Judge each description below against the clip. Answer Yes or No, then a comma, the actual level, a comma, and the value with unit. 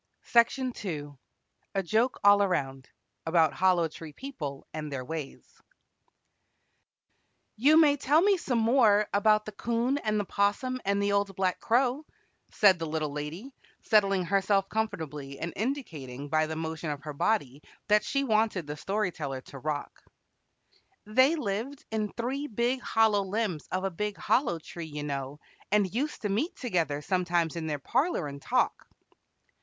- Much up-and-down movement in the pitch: Yes, wide, 6.6 semitones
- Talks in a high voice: Yes, high, 195 Hz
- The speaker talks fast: No, average, 160 wpm